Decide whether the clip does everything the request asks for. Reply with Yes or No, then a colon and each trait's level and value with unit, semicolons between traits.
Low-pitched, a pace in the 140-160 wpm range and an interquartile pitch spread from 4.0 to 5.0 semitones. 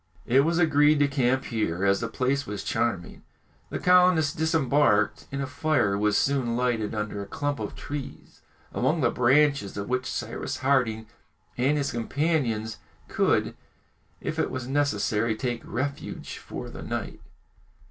Yes: low, 130 Hz; average, 150 wpm; average, 4.5 semitones